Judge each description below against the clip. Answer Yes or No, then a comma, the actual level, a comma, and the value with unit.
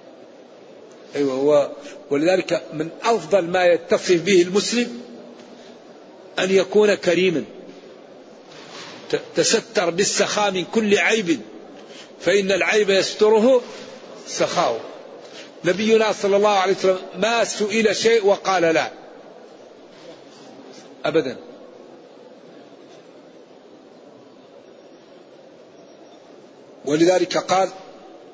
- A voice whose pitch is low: No, high, 200 Hz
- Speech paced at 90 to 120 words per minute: No, average, 70 wpm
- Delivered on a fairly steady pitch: No, average, 3.8 semitones